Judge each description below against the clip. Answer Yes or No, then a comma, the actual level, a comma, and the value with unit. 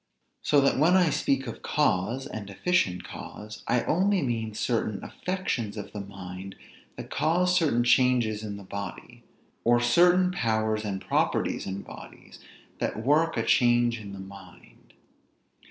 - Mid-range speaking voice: No, low, 115 Hz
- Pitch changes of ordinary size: No, wide, 6.5 semitones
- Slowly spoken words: No, average, 150 wpm